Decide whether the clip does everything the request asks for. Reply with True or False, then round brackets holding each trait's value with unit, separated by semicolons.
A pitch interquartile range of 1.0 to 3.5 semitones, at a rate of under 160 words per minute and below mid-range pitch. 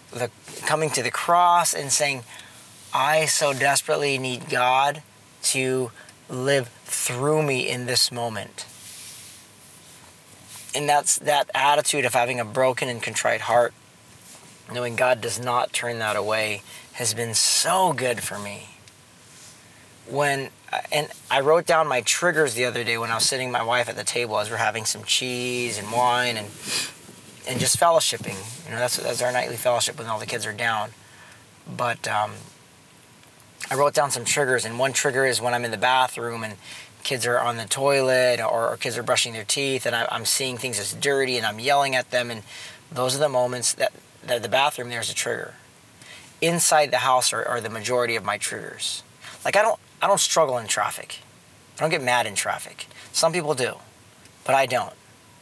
False (2.8 semitones; 185 wpm; 125 Hz)